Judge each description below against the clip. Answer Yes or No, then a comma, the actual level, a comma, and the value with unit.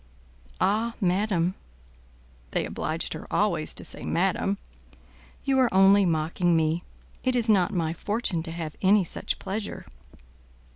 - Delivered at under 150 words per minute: Yes, slow, 135 wpm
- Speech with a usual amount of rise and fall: Yes, average, 4.2 semitones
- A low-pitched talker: No, medium, 185 Hz